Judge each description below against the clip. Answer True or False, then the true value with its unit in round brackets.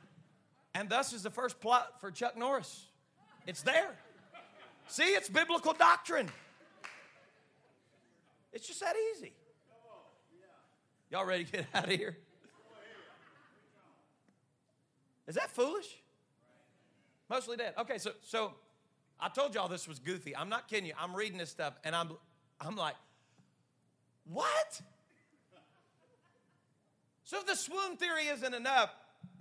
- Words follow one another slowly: True (120 wpm)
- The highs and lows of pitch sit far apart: True (8.1 semitones)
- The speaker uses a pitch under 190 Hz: False (215 Hz)